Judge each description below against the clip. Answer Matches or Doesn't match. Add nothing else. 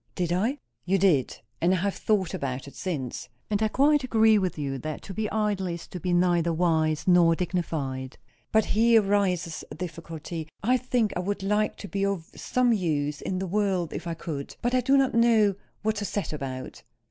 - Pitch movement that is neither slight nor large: Matches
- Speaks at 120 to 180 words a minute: Doesn't match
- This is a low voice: Doesn't match